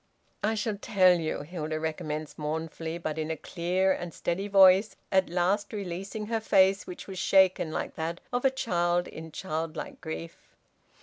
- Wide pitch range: No, average, 3.4 semitones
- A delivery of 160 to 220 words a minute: Yes, average, 165 wpm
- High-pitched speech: No, medium, 175 Hz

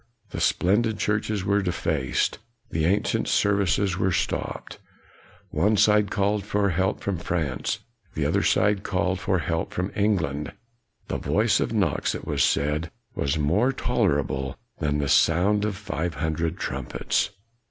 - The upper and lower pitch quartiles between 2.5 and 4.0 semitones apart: No, average, 4.4 semitones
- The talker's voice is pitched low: Yes, very low, 95 Hz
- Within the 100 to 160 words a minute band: Yes, average, 150 wpm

